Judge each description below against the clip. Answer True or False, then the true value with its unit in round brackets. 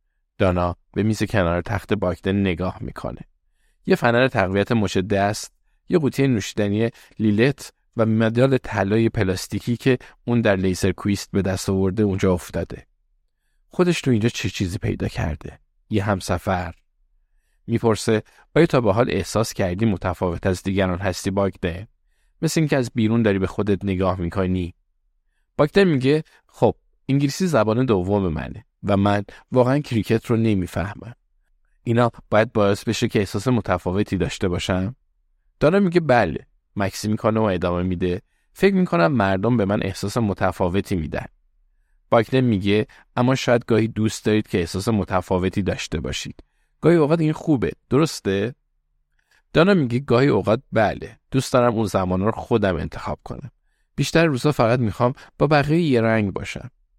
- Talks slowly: False (145 wpm)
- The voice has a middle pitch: False (105 Hz)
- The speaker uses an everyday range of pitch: True (4.3 semitones)